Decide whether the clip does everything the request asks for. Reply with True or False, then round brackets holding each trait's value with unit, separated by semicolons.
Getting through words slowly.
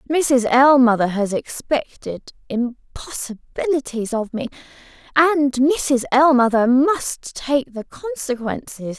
True (95 wpm)